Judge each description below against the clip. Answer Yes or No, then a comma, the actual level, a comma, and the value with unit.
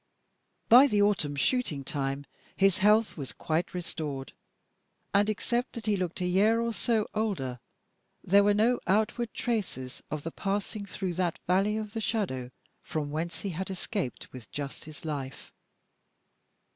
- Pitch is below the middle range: No, high, 195 Hz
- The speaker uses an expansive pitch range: Yes, wide, 6.0 semitones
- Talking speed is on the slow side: No, average, 155 wpm